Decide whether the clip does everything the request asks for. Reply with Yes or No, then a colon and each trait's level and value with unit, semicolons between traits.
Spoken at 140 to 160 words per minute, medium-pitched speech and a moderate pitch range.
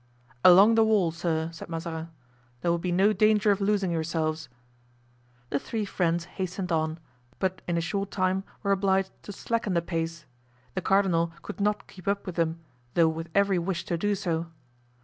No: average, 180 wpm; medium, 180 Hz; average, 3.1 semitones